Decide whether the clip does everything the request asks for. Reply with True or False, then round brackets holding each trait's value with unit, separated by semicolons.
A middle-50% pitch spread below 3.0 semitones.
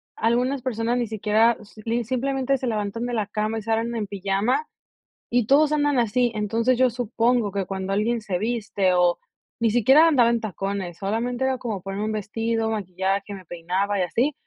False (3.4 semitones)